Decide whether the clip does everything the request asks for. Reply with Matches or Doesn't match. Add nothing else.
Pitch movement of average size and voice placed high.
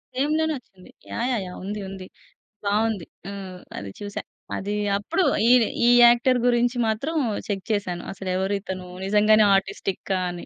Matches